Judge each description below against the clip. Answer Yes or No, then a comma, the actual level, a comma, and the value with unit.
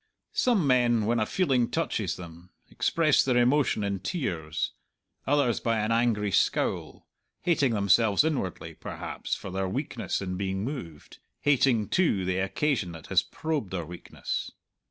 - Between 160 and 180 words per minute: No, average, 145 wpm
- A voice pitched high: No, low, 110 Hz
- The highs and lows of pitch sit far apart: Yes, wide, 6.4 semitones